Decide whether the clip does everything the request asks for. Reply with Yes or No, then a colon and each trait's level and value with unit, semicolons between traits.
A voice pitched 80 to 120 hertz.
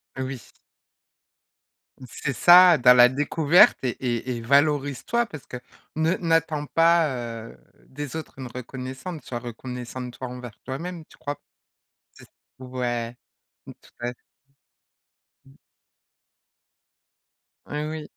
No: low, 135 Hz